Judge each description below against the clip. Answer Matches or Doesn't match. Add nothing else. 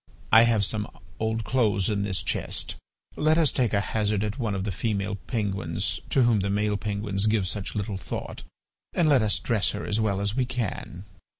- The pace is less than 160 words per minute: Doesn't match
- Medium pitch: Doesn't match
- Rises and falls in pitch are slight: Matches